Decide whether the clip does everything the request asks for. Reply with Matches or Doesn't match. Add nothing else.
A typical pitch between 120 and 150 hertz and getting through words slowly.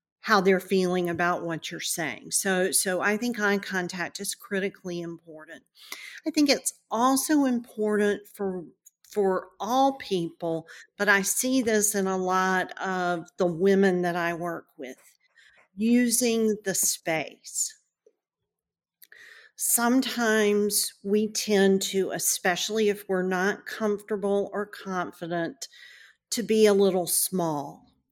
Doesn't match